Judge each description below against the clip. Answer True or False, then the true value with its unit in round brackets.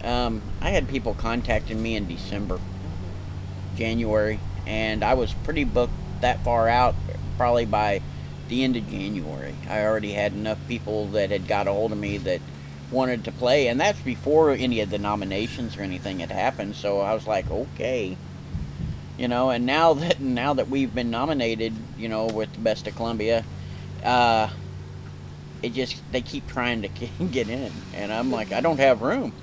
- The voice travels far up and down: False (4.4 semitones)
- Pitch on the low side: True (110 Hz)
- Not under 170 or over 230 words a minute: True (180 wpm)